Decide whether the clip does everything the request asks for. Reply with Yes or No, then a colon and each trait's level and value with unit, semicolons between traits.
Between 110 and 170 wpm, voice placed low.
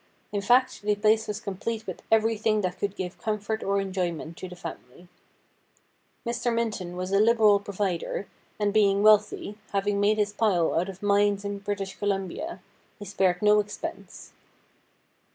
No: average, 165 wpm; high, 205 Hz